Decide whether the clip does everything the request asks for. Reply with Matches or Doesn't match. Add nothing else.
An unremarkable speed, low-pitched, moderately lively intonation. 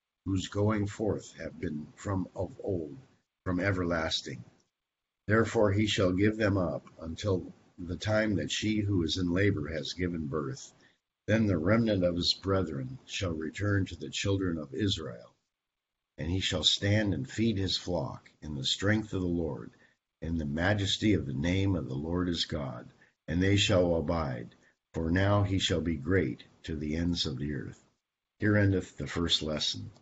Matches